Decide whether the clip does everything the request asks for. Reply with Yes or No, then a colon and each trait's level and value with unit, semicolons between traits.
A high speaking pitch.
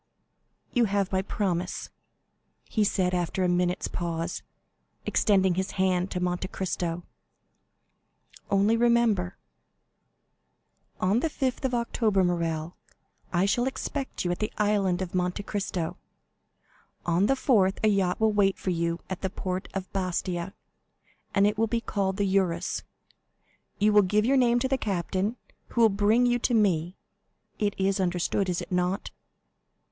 Yes: high, 195 Hz